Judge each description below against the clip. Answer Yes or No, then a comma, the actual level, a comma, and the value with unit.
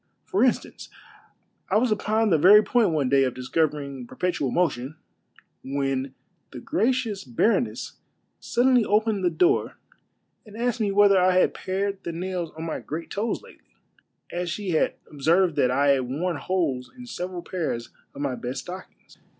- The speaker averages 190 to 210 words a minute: No, average, 165 wpm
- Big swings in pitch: Yes, wide, 6.7 semitones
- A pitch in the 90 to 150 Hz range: No, medium, 180 Hz